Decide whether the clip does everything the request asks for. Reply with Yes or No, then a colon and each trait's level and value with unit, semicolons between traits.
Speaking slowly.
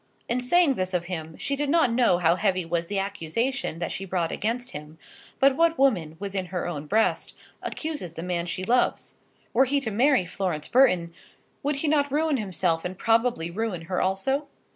No: average, 190 wpm